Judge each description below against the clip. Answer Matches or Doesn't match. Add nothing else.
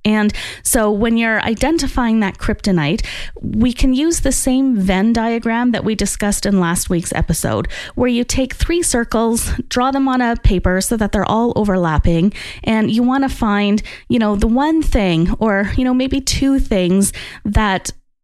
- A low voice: Doesn't match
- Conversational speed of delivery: Matches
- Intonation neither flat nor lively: Matches